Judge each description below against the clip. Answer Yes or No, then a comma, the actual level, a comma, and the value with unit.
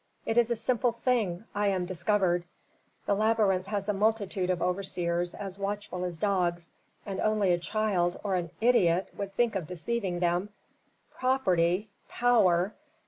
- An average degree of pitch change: Yes, average, 3.3 semitones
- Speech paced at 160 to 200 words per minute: No, average, 150 wpm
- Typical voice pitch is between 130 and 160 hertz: No, high, 195 Hz